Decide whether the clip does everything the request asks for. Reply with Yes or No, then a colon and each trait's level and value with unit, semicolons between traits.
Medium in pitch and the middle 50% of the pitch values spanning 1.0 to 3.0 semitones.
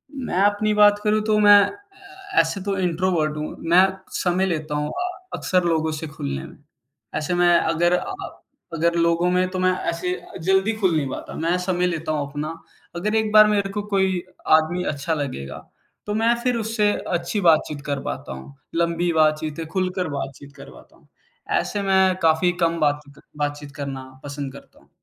No: medium, 175 Hz; average, 4.2 semitones